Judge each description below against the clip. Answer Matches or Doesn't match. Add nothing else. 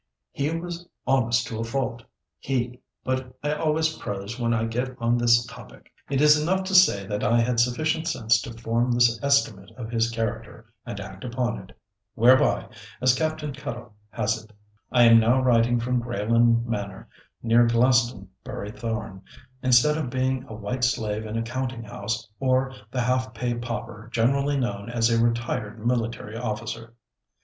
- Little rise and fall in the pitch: Matches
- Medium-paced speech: Matches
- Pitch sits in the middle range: Doesn't match